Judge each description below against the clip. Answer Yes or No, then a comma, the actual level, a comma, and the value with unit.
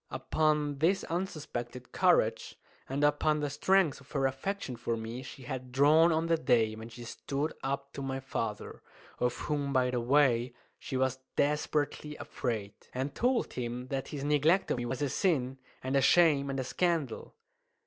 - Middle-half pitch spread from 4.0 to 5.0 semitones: No, average, 3.2 semitones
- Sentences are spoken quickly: No, average, 175 wpm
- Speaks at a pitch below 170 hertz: Yes, low, 135 Hz